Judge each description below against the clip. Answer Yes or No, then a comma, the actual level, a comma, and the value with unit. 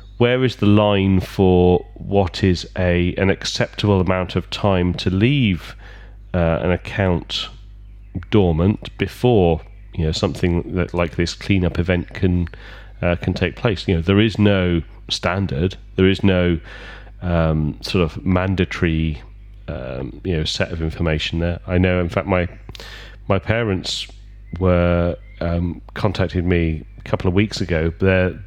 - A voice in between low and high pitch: No, very low, 95 Hz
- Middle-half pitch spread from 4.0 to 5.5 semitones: No, average, 2.7 semitones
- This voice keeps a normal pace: Yes, average, 150 wpm